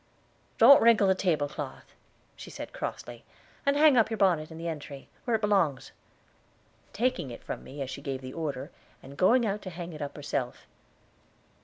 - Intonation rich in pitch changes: Yes, wide, 7.2 semitones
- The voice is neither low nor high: Yes, medium, 170 Hz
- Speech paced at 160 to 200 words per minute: Yes, average, 180 wpm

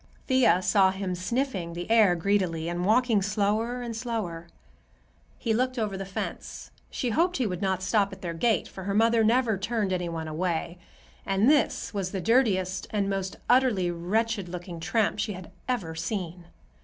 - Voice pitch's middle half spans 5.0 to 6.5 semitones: No, average, 4.2 semitones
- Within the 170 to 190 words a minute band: Yes, average, 175 wpm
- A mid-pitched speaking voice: No, high, 195 Hz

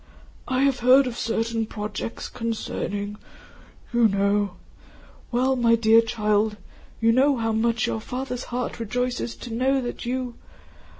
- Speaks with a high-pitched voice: Yes, high, 230 Hz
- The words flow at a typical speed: No, slow, 130 wpm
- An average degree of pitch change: No, narrow, 2.3 semitones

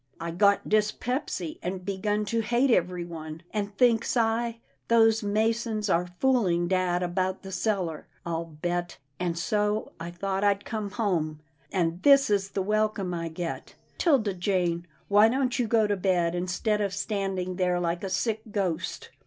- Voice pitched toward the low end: No, high, 195 Hz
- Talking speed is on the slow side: No, average, 165 wpm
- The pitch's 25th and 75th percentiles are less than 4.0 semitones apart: Yes, average, 3.6 semitones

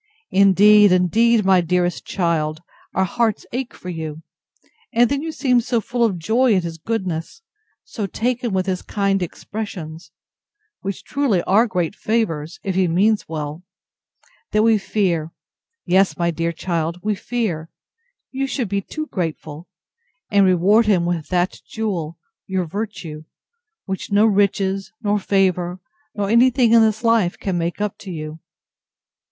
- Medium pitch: No, high, 195 Hz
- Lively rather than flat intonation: No, average, 4.3 semitones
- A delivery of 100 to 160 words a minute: Yes, average, 145 wpm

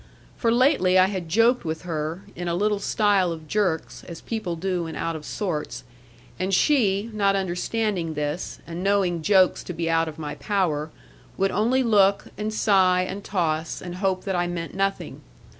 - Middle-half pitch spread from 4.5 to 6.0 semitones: No, average, 3.4 semitones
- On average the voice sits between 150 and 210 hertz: Yes, medium, 185 Hz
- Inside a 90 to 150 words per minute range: No, average, 180 wpm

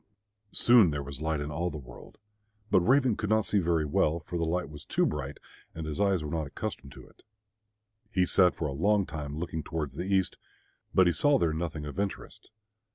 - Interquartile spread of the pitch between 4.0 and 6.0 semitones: Yes, average, 4.4 semitones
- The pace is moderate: No, fast, 210 wpm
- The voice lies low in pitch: Yes, very low, 85 Hz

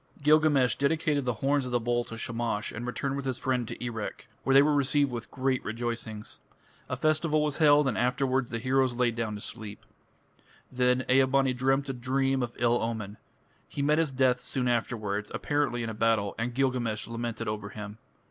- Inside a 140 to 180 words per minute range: No, average, 195 wpm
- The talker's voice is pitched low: Yes, low, 125 Hz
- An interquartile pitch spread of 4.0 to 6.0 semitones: No, average, 2.8 semitones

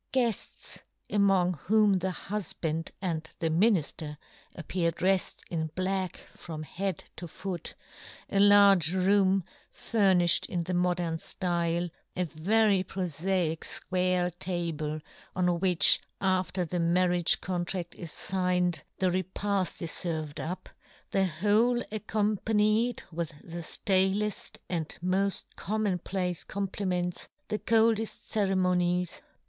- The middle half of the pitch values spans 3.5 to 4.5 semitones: No, narrow, 2.4 semitones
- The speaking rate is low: Yes, slow, 125 wpm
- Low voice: No, medium, 185 Hz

